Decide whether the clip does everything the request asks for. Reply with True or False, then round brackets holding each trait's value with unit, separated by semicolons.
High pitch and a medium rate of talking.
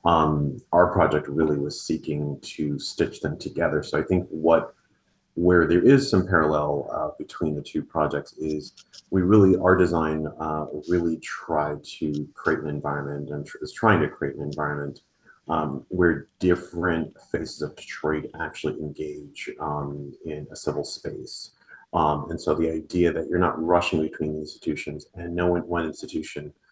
False (75 Hz; 165 wpm)